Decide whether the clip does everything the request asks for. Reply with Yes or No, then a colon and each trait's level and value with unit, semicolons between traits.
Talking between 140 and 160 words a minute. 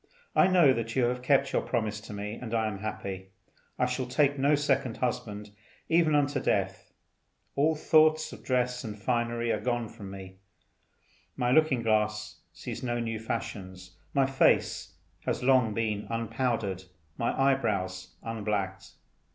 Yes: average, 150 wpm